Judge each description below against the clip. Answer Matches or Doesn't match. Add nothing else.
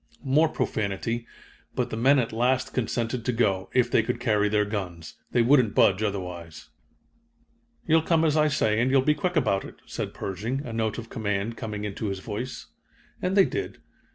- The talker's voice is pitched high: Doesn't match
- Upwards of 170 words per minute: Matches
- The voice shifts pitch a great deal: Doesn't match